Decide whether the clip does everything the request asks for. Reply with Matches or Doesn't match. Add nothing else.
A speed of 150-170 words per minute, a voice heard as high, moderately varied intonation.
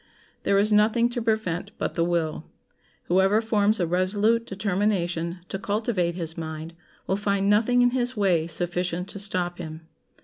Matches